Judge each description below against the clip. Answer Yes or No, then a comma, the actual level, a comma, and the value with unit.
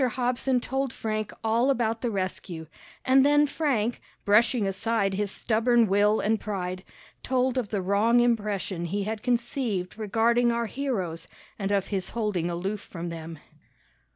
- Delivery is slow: No, average, 150 wpm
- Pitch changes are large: No, average, 3.6 semitones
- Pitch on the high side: Yes, high, 215 Hz